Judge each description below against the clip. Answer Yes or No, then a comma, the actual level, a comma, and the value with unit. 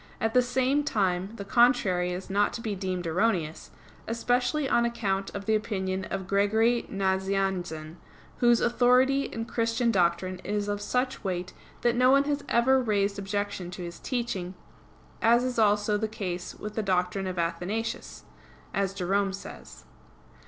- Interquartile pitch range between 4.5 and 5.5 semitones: No, average, 4.0 semitones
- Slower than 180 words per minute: Yes, average, 155 wpm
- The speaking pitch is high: Yes, high, 205 Hz